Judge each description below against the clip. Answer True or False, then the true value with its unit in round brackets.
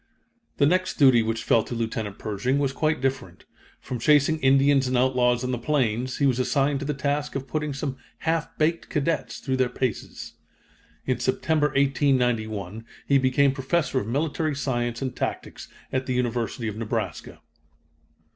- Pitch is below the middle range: True (130 Hz)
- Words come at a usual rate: True (165 wpm)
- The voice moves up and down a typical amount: True (3.0 semitones)